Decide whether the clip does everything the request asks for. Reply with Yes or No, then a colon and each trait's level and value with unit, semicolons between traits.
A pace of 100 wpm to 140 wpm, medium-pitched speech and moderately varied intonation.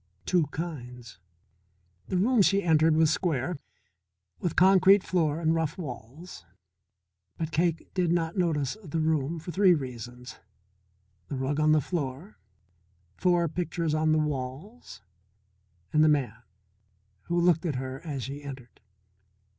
Yes: slow, 135 wpm; medium, 155 Hz; average, 4.2 semitones